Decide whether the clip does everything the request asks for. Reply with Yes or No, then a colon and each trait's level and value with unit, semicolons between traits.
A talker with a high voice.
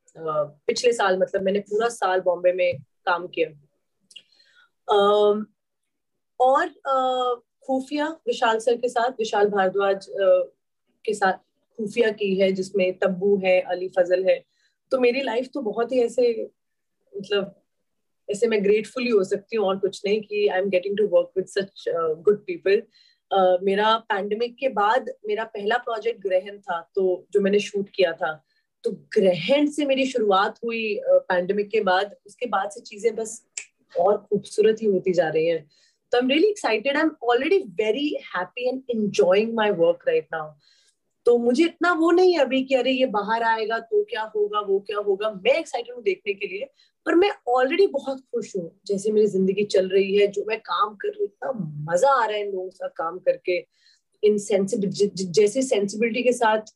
Yes: high, 220 Hz